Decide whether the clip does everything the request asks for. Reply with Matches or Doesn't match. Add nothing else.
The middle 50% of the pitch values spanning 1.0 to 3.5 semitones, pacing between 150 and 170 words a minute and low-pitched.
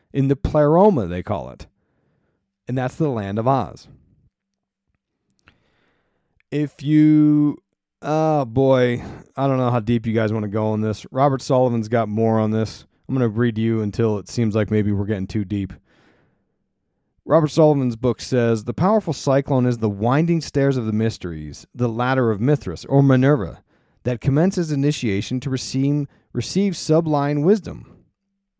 Doesn't match